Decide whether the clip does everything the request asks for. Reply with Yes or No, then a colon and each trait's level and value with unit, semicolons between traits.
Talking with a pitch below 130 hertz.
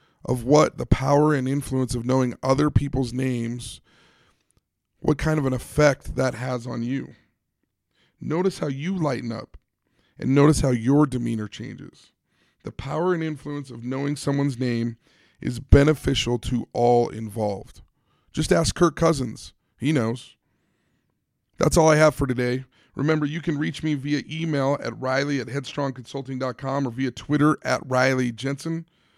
No: low, 135 Hz